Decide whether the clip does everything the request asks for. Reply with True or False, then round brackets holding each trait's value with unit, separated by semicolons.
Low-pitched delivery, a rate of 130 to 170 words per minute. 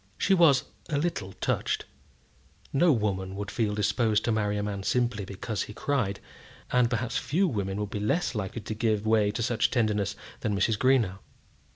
False (110 Hz; 180 wpm)